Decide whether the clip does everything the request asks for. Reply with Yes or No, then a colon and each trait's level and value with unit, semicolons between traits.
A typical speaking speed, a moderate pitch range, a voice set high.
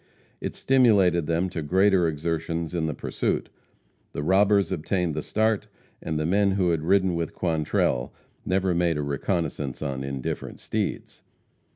No: average, 150 wpm; average, 3.8 semitones; very low, 85 Hz